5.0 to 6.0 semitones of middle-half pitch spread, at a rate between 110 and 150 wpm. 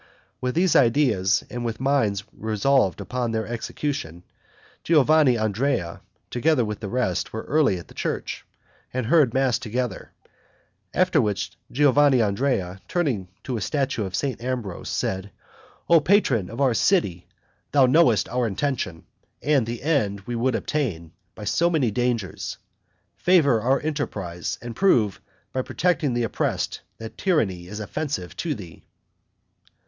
Yes: wide, 5.5 semitones; average, 140 wpm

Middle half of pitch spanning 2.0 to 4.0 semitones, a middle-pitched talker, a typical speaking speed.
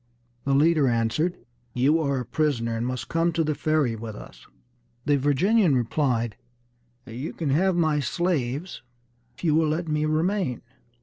No: average, 4.5 semitones; medium, 150 Hz; average, 160 wpm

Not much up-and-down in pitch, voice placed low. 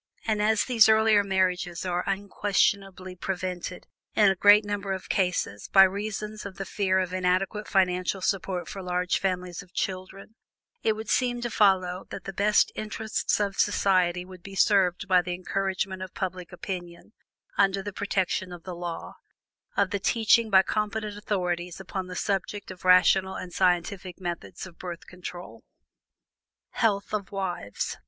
No: narrow, 2.0 semitones; high, 190 Hz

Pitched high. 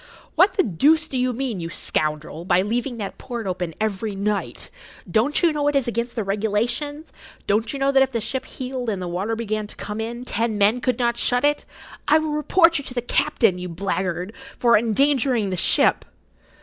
Yes: high, 230 Hz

